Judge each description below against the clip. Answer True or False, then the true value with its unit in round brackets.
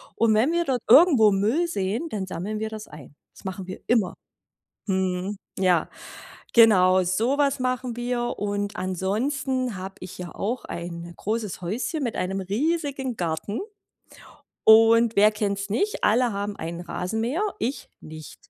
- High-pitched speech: True (210 Hz)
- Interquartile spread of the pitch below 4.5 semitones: False (4.8 semitones)